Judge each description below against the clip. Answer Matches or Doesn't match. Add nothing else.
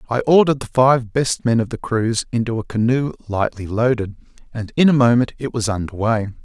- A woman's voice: Doesn't match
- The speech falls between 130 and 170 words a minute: Doesn't match